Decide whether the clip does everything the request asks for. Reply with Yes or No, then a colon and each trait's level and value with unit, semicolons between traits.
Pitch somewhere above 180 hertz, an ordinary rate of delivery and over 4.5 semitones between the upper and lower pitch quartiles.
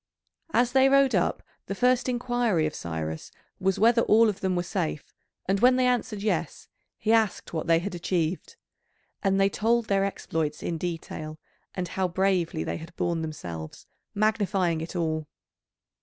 Yes: high, 190 Hz; average, 165 wpm; average, 5.2 semitones